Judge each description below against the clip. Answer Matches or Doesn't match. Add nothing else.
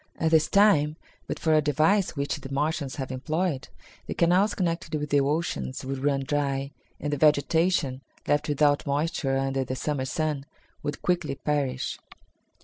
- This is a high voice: Doesn't match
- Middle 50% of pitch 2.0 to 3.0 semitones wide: Matches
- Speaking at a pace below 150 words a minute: Doesn't match